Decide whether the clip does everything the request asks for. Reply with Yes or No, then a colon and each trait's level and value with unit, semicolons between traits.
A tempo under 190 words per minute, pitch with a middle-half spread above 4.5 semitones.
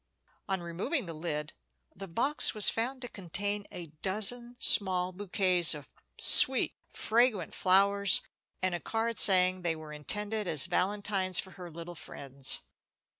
No: average, 140 wpm; average, 3.3 semitones